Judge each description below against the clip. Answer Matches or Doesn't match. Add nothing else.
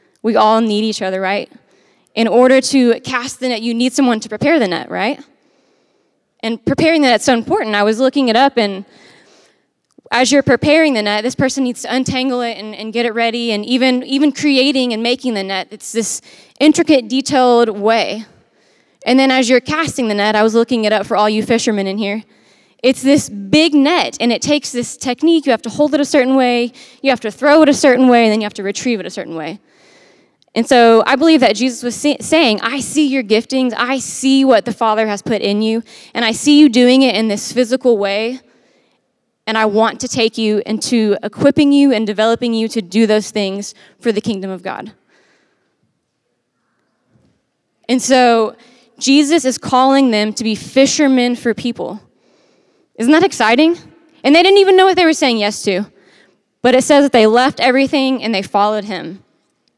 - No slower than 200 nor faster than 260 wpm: Matches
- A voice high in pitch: Matches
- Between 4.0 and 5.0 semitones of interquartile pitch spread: Doesn't match